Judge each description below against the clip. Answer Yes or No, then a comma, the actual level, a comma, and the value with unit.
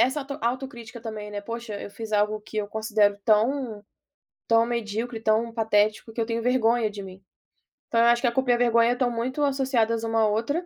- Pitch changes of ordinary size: No, narrow, 2.1 semitones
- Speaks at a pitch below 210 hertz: No, high, 230 Hz